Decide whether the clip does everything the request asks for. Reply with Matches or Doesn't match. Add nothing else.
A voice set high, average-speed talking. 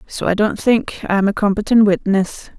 Matches